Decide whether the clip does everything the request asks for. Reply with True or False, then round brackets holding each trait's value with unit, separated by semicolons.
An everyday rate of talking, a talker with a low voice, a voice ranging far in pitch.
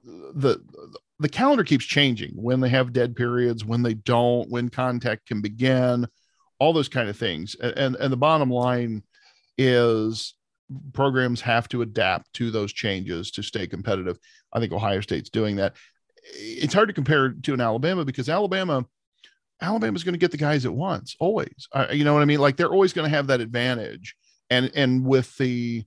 False (190 wpm; 125 Hz; 4.1 semitones)